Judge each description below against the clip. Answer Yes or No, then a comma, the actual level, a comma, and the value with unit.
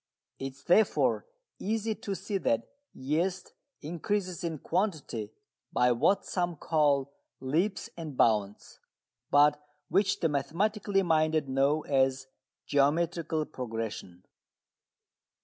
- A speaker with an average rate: No, slow, 105 wpm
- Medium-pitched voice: Yes, medium, 155 Hz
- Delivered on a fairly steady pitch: No, average, 5.2 semitones